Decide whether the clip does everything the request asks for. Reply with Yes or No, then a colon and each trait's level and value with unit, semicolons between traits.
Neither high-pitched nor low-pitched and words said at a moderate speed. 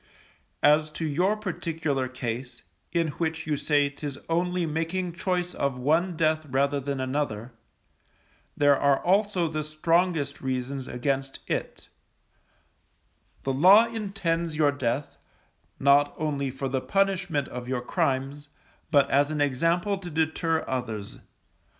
No: medium, 150 Hz; slow, 130 wpm